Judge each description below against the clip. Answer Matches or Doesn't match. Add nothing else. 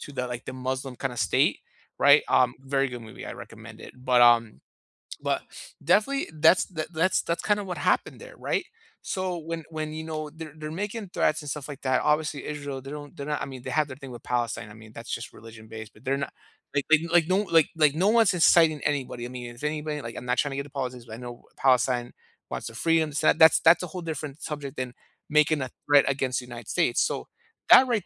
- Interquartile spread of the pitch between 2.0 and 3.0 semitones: Doesn't match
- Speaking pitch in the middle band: Matches